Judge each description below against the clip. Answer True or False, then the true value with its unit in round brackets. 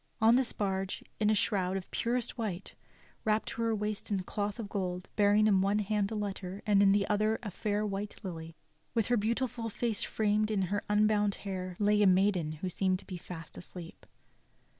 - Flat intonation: True (2.1 semitones)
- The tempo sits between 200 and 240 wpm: True (205 wpm)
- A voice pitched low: False (205 Hz)